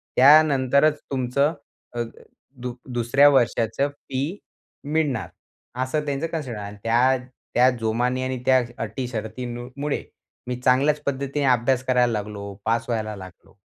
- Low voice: Yes, low, 130 Hz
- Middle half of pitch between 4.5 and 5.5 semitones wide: No, average, 3.1 semitones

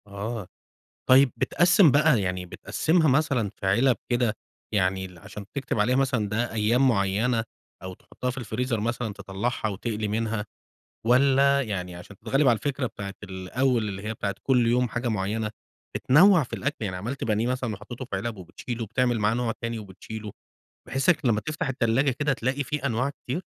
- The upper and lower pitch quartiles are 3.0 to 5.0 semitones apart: Yes, average, 4.1 semitones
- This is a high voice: No, low, 115 Hz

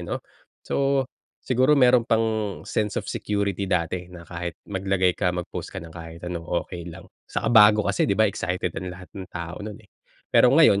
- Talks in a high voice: No, very low, 95 Hz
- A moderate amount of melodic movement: Yes, average, 3.2 semitones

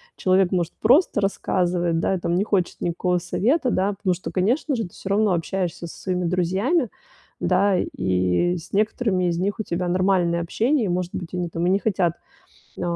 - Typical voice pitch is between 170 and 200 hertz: Yes, medium, 185 Hz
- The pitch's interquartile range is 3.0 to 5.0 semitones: No, narrow, 2.6 semitones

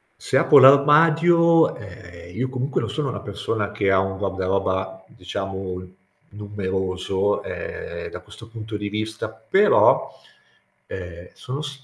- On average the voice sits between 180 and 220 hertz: No, low, 105 Hz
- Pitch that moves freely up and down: Yes, wide, 5.7 semitones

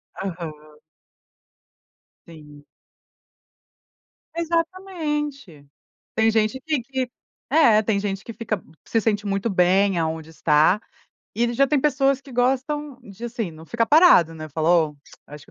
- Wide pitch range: Yes, wide, 8.0 semitones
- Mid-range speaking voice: No, high, 220 Hz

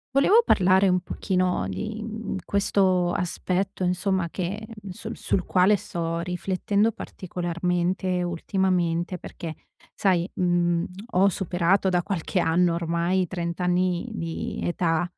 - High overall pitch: No, medium, 180 Hz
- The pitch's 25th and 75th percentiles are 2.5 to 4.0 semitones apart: No, narrow, 1.7 semitones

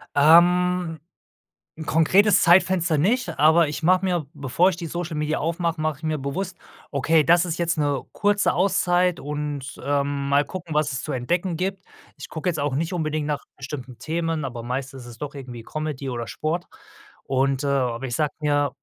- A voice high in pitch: No, medium, 155 Hz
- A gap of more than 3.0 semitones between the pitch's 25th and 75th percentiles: Yes, average, 3.7 semitones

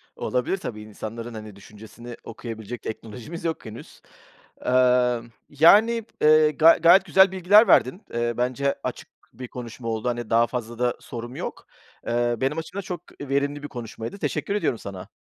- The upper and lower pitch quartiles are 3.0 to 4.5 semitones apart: No, average, 5.2 semitones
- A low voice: Yes, low, 125 Hz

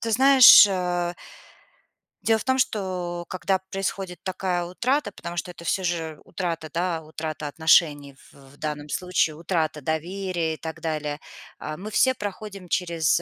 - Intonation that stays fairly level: No, average, 3.3 semitones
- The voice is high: No, medium, 175 Hz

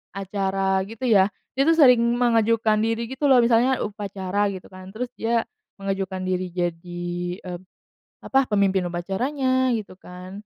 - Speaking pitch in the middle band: No, high, 205 Hz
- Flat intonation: No, average, 4.0 semitones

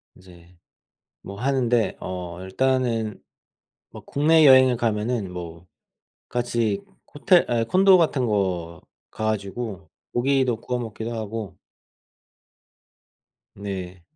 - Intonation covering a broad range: No, average, 5.0 semitones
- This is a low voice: Yes, low, 110 Hz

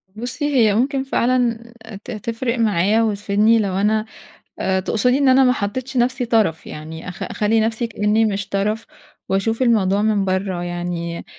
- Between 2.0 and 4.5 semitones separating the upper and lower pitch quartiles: Yes, average, 3.3 semitones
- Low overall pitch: No, high, 215 Hz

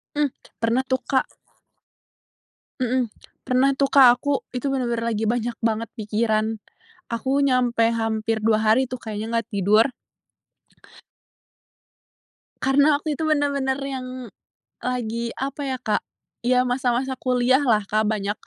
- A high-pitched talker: Yes, high, 245 Hz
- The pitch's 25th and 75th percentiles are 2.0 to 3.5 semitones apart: Yes, average, 3.0 semitones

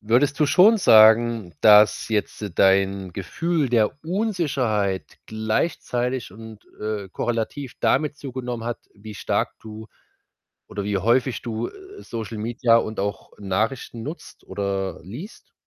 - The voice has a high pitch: No, low, 115 Hz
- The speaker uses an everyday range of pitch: Yes, average, 3.9 semitones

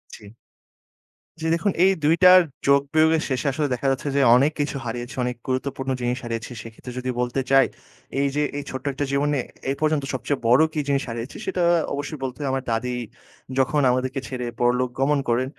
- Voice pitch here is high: No, low, 135 Hz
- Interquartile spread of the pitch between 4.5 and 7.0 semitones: No, average, 2.7 semitones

